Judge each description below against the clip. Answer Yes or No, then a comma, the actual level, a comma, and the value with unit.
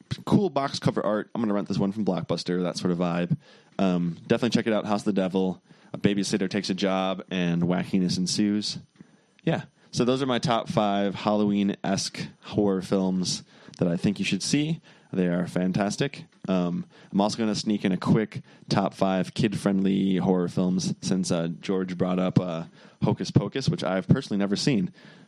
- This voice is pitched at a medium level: No, low, 100 Hz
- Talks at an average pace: Yes, average, 190 wpm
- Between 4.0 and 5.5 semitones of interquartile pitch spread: No, average, 2.7 semitones